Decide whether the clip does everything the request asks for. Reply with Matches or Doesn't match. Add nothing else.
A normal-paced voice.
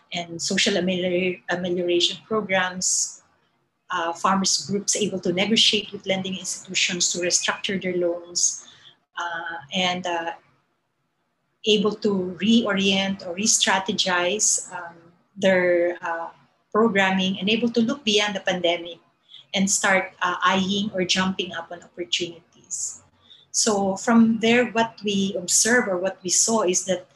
Doesn't match